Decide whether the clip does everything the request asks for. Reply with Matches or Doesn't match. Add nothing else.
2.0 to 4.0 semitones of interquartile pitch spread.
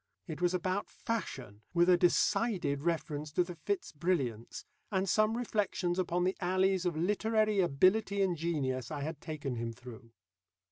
Doesn't match